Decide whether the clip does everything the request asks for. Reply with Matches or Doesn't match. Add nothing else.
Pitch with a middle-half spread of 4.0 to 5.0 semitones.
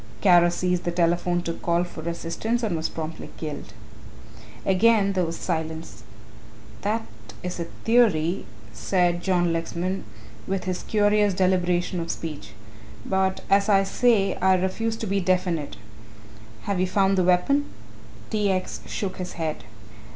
Doesn't match